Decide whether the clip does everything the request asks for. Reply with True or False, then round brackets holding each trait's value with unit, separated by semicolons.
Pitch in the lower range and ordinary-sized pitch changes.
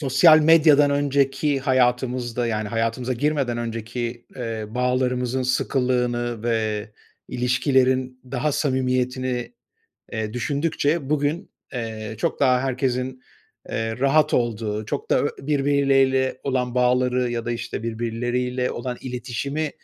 False (125 Hz; 2.2 semitones)